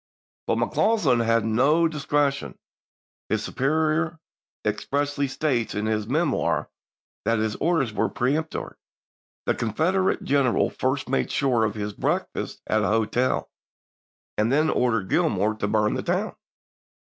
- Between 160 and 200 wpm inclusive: No, slow, 135 wpm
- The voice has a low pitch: Yes, low, 130 Hz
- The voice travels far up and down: Yes, wide, 5.9 semitones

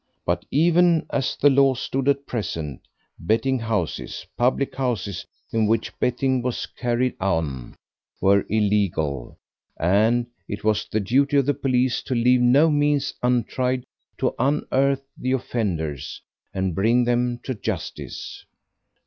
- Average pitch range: Yes, average, 4.7 semitones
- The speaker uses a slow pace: Yes, slow, 130 wpm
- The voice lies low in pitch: Yes, low, 120 Hz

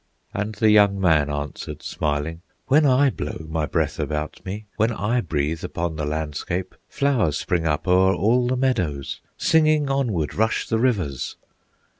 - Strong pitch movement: Yes, wide, 7.5 semitones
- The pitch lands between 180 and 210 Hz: No, very low, 95 Hz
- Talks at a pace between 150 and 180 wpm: Yes, average, 155 wpm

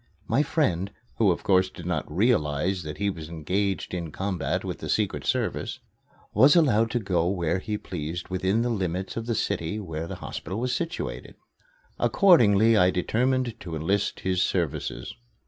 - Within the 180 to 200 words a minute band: No, average, 165 wpm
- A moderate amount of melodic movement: Yes, average, 4.8 semitones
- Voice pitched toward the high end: No, very low, 95 Hz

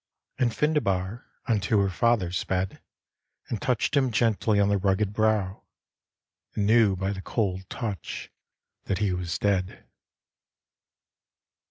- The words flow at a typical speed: No, slow, 130 wpm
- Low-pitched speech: Yes, low, 100 Hz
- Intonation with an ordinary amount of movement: Yes, average, 3.0 semitones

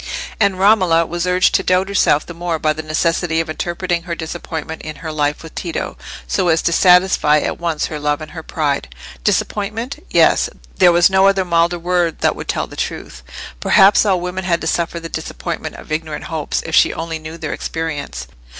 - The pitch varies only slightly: Yes, narrow, 2.3 semitones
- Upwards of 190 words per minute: Yes, average, 200 wpm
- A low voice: No, medium, 170 Hz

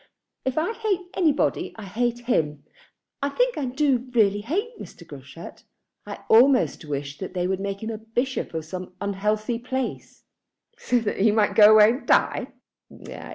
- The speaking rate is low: No, average, 160 wpm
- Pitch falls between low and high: No, high, 225 Hz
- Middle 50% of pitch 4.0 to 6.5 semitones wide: Yes, average, 5.2 semitones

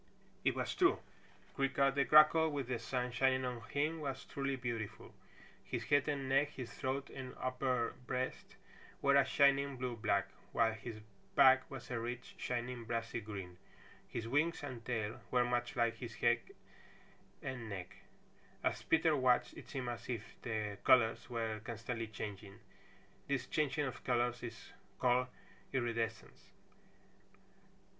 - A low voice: Yes, low, 125 Hz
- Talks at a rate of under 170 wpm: Yes, average, 145 wpm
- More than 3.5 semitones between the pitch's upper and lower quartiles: No, average, 3.0 semitones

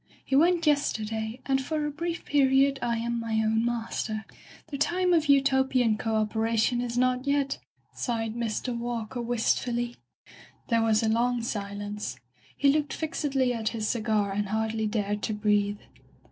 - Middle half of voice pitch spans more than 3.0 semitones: Yes, average, 3.6 semitones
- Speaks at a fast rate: No, average, 155 wpm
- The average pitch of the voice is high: Yes, high, 235 Hz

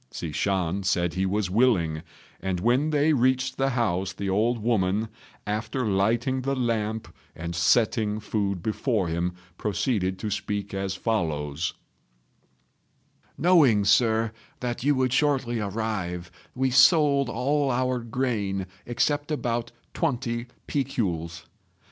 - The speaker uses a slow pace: Yes, slow, 125 wpm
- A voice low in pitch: Yes, low, 110 Hz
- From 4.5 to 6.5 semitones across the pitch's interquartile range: Yes, average, 5.0 semitones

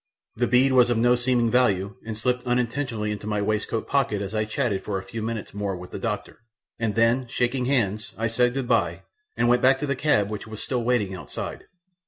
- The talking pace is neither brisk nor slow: No, fast, 215 wpm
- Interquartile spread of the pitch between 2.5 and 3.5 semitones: Yes, average, 2.9 semitones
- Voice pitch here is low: Yes, low, 115 Hz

